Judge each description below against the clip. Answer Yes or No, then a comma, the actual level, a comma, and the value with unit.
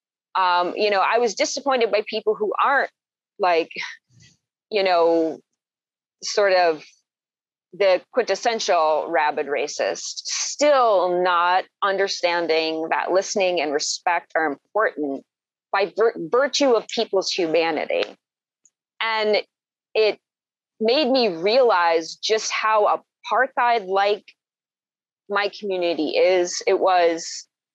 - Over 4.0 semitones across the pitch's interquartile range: Yes, average, 4.5 semitones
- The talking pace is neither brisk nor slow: No, slow, 105 wpm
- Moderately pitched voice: No, high, 195 Hz